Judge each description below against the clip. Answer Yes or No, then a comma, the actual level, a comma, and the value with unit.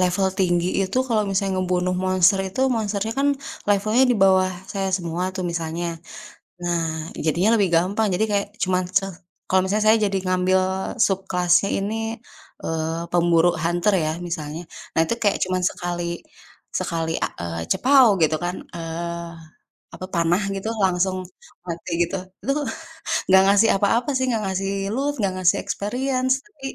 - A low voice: No, medium, 185 Hz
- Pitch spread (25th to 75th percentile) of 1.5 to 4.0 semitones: Yes, average, 2.9 semitones